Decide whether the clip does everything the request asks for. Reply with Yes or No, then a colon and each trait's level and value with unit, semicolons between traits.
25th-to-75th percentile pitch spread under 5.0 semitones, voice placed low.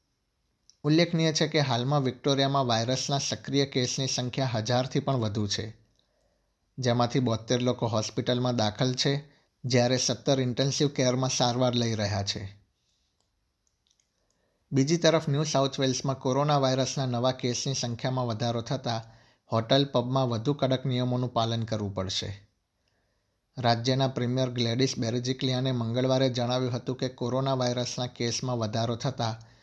Yes: average, 2.8 semitones; low, 125 Hz